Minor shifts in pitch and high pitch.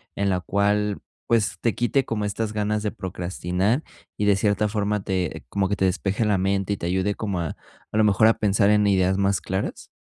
No: narrow, 1.9 semitones; low, 100 Hz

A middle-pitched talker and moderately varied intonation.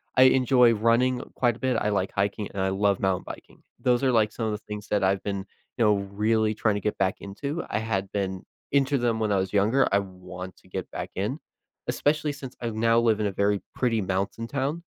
No: low, 105 Hz; average, 3.6 semitones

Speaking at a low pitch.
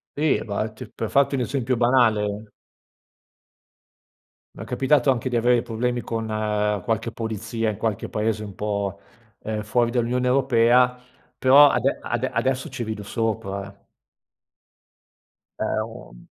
Yes: low, 115 Hz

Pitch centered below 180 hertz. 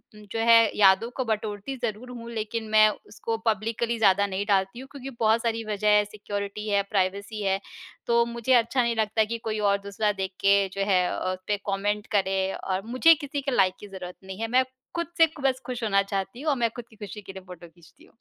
No: high, 215 Hz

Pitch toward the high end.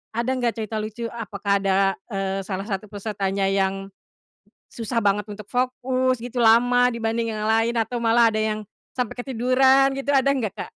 Yes: high, 225 Hz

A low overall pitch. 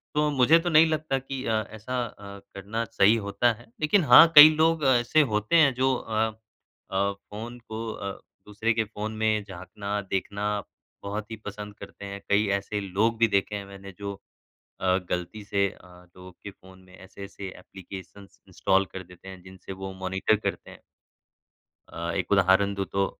Yes: low, 105 Hz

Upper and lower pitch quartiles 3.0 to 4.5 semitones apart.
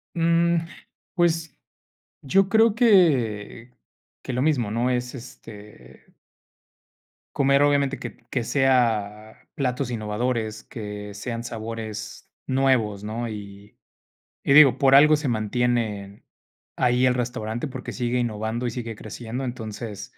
Yes: average, 3.7 semitones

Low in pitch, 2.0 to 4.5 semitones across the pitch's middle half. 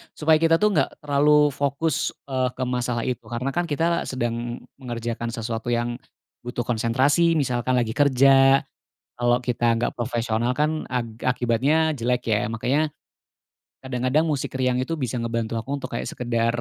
Yes: low, 125 Hz; average, 3.2 semitones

